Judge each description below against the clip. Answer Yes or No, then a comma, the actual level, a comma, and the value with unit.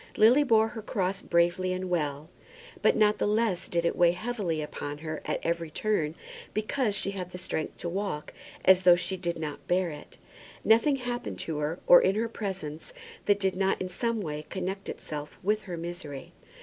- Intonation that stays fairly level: No, average, 4.1 semitones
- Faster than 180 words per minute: Yes, average, 190 wpm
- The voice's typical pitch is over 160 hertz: Yes, medium, 185 Hz